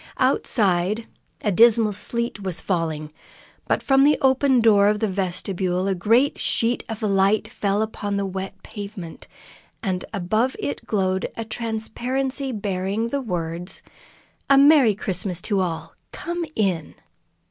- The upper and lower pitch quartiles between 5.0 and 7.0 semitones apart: No, average, 3.8 semitones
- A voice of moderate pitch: No, high, 205 Hz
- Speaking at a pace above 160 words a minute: No, slow, 135 wpm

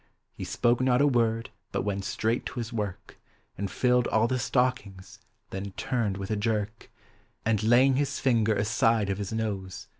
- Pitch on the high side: No, low, 110 Hz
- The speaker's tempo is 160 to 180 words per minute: Yes, average, 175 wpm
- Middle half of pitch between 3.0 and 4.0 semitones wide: Yes, average, 3.4 semitones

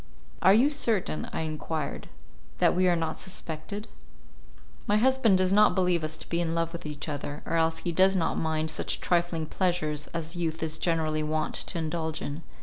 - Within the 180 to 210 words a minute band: Yes, average, 190 wpm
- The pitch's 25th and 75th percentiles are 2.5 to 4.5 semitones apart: Yes, average, 2.8 semitones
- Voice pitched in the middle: Yes, medium, 165 Hz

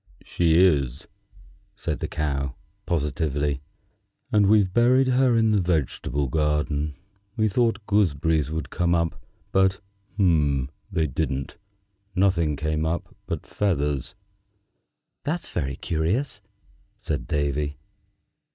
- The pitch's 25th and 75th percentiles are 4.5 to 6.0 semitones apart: Yes, average, 5.3 semitones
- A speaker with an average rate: No, slow, 105 wpm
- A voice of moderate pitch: No, very low, 80 Hz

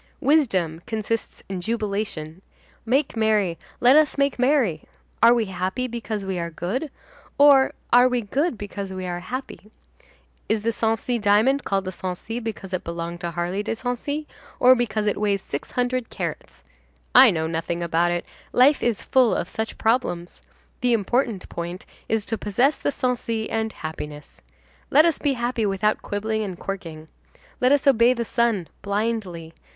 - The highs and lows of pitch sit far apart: No, average, 5.0 semitones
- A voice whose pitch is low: No, high, 220 Hz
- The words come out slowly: No, average, 165 wpm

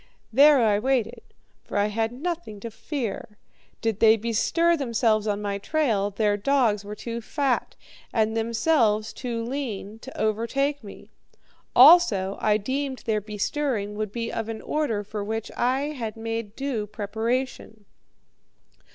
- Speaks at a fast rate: No, average, 145 wpm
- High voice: Yes, high, 225 Hz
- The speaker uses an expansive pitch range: No, average, 3.9 semitones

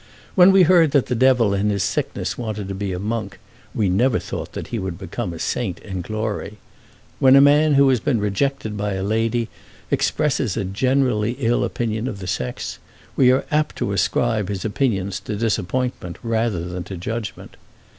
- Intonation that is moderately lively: Yes, average, 4.6 semitones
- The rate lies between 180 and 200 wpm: Yes, average, 185 wpm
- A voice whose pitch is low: Yes, low, 110 Hz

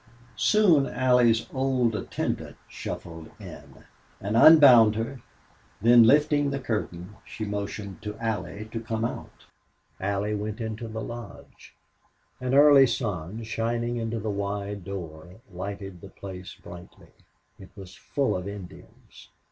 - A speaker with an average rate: No, slow, 115 wpm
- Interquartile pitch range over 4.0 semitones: No, average, 3.3 semitones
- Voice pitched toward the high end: No, low, 110 Hz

